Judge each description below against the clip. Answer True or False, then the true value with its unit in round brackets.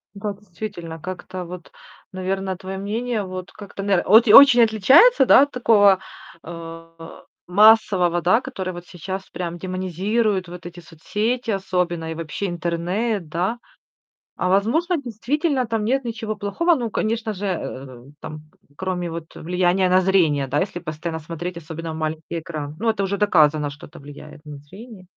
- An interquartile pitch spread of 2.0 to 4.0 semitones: False (4.4 semitones)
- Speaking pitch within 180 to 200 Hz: True (185 Hz)